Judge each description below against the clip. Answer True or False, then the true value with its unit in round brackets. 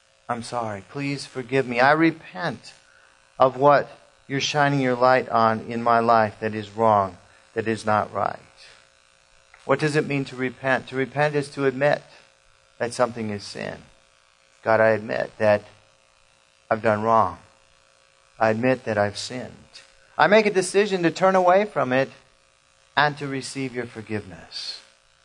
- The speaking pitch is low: True (110 Hz)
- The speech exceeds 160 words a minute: False (155 wpm)